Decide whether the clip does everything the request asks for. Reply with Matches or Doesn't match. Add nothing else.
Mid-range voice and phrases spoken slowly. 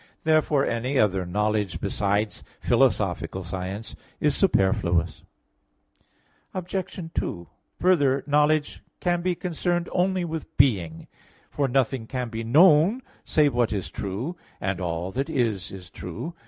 Doesn't match